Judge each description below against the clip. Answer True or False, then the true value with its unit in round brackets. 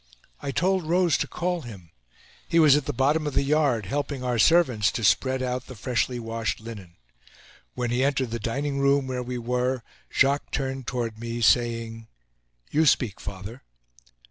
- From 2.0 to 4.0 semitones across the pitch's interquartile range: True (3.6 semitones)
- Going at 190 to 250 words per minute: False (170 wpm)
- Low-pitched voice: True (125 Hz)